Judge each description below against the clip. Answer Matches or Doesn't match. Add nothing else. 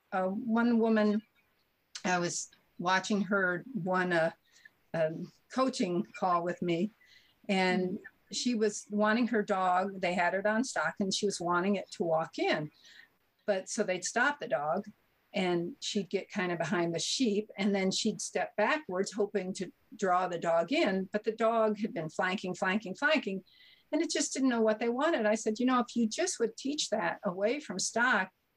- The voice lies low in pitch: Doesn't match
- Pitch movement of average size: Matches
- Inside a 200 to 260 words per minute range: Doesn't match